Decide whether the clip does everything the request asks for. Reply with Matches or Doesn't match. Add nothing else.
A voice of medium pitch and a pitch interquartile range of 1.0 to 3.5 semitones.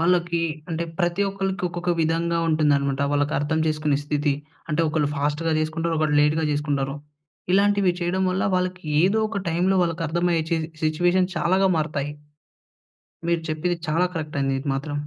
Matches